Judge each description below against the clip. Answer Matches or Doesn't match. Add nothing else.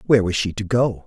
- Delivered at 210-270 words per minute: Doesn't match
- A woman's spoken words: Doesn't match